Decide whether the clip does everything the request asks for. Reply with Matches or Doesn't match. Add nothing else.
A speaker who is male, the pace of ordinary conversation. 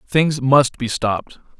Matches